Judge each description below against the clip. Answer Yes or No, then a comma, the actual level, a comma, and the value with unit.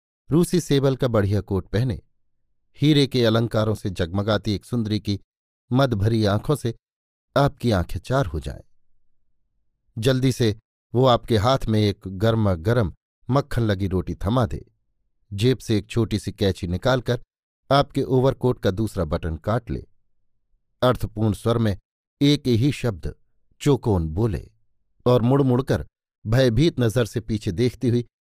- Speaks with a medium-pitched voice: No, low, 115 Hz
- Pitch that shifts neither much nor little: Yes, average, 3.5 semitones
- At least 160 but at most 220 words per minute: No, average, 145 wpm